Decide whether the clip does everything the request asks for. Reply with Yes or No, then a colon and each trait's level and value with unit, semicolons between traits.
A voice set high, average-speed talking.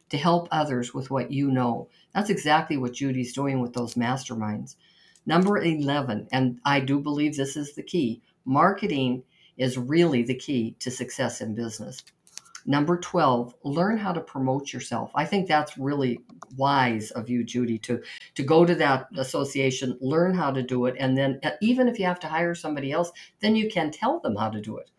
No: low, 135 Hz; average, 190 wpm